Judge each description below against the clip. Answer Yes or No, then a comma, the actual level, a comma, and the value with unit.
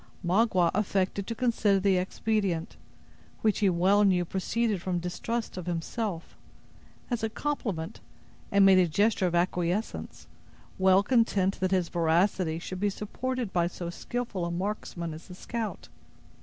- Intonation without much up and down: No, average, 3.4 semitones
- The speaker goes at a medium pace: Yes, average, 145 wpm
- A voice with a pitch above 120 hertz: Yes, high, 190 Hz